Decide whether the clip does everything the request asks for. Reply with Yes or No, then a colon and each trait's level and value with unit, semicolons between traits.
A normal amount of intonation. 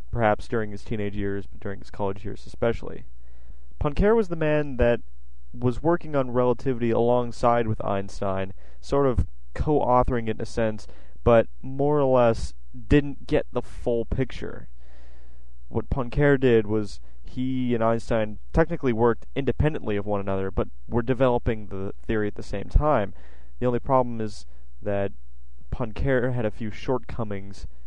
No: wide, 5.8 semitones